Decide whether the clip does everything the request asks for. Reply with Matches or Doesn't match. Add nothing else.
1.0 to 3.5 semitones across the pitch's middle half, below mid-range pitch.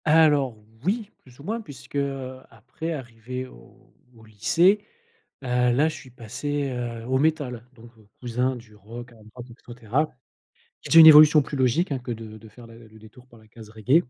Doesn't match